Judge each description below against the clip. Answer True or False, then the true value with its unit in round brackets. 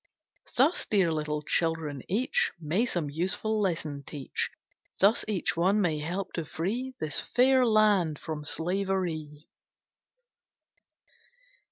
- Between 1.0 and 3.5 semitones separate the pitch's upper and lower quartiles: False (5.6 semitones)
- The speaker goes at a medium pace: False (115 wpm)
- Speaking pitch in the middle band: True (175 Hz)